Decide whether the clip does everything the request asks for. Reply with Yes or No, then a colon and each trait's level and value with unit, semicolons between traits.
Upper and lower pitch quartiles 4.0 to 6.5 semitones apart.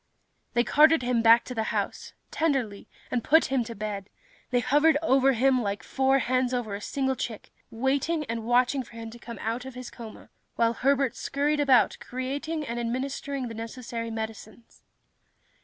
No: average, 2.9 semitones